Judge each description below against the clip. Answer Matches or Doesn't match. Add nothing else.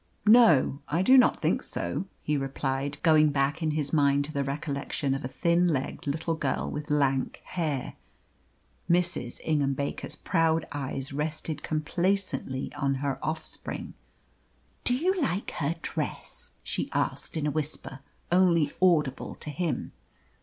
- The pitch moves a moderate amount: Matches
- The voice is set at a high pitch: Doesn't match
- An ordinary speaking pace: Matches